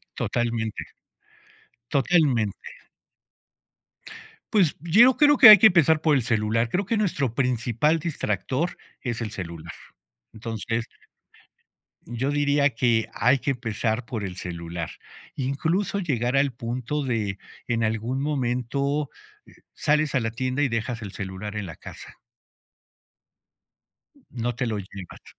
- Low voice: Yes, low, 125 Hz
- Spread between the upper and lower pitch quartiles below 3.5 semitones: No, average, 4.7 semitones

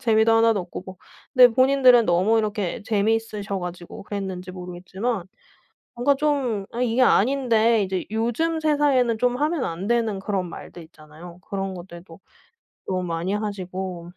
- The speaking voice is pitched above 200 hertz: Yes, high, 210 Hz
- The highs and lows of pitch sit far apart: No, average, 4.7 semitones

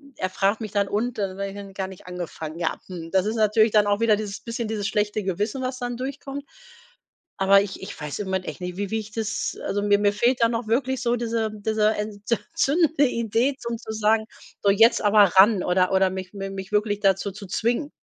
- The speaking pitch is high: Yes, high, 210 Hz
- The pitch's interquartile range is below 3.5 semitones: Yes, average, 2.9 semitones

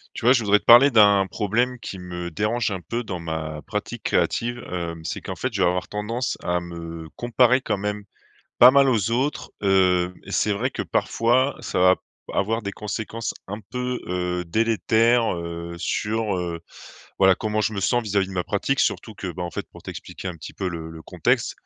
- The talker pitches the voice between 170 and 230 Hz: No, low, 100 Hz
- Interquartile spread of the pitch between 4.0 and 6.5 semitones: Yes, average, 4.6 semitones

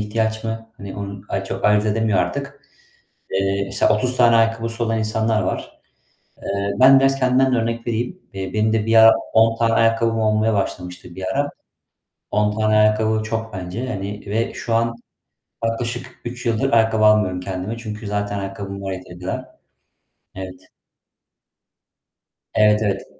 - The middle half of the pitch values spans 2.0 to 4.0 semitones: Yes, narrow, 2.4 semitones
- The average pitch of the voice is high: No, low, 110 Hz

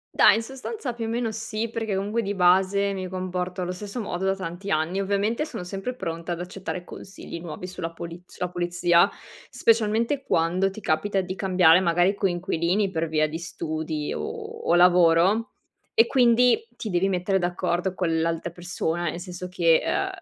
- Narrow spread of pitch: No, average, 3.1 semitones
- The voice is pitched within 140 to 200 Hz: Yes, medium, 185 Hz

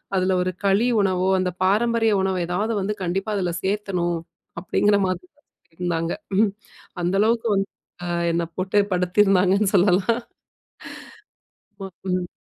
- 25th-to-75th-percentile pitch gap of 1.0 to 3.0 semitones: Yes, narrow, 2.4 semitones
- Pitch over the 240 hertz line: No, high, 190 Hz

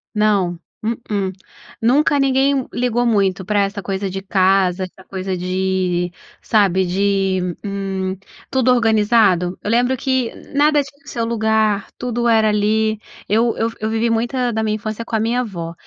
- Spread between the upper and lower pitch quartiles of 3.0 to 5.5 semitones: Yes, average, 3.6 semitones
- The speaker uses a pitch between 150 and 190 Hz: No, high, 215 Hz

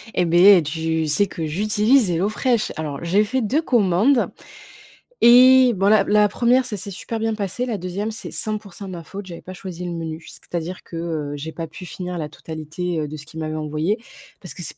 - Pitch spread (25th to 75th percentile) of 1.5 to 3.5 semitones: No, average, 4.7 semitones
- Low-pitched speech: No, medium, 180 Hz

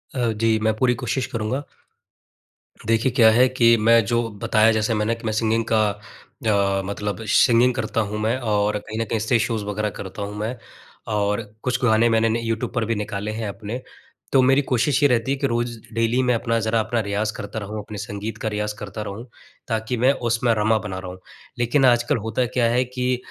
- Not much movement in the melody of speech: Yes, narrow, 2.2 semitones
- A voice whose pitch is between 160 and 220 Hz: No, low, 115 Hz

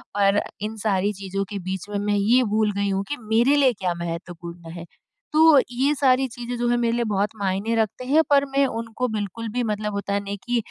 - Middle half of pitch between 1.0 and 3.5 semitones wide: No, average, 3.9 semitones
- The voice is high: Yes, high, 215 Hz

